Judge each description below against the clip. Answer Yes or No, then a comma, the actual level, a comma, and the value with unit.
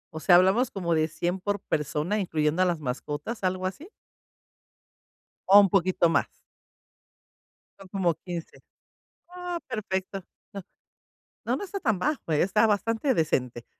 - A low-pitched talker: No, medium, 185 Hz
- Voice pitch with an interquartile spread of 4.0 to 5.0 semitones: Yes, average, 4.3 semitones